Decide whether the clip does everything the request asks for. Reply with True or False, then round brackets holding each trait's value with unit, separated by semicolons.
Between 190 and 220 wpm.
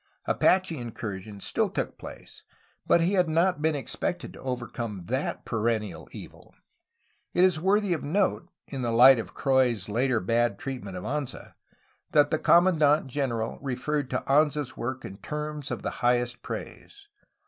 False (160 wpm)